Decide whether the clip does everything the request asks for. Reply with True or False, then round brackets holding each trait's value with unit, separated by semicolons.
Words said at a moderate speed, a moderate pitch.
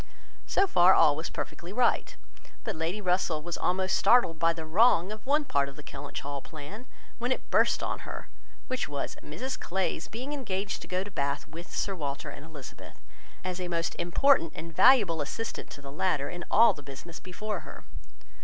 True (190 wpm; 175 Hz)